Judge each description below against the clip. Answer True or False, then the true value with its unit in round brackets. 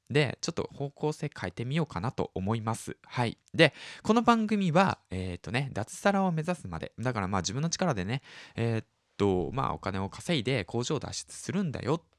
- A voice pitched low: True (130 Hz)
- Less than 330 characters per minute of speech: False (375 characters per minute)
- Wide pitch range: True (9.0 semitones)